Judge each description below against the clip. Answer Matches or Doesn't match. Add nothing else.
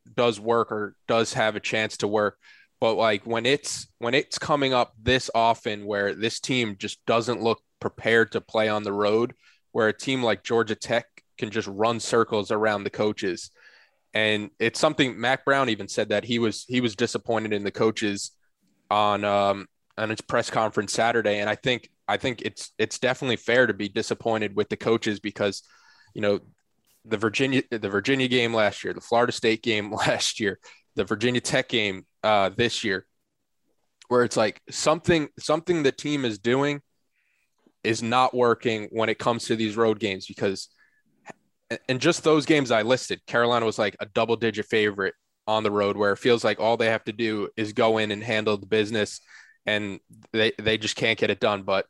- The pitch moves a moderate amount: Doesn't match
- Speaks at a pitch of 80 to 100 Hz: Doesn't match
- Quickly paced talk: Doesn't match